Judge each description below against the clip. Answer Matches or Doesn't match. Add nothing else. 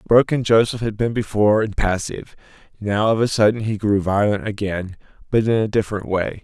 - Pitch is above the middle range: Doesn't match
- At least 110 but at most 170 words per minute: Doesn't match